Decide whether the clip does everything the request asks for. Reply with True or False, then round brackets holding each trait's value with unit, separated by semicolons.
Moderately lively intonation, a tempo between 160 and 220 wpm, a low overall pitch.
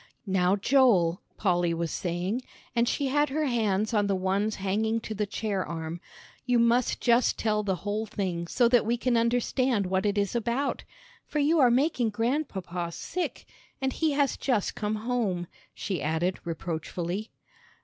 False (4.7 semitones; 165 wpm; 215 Hz)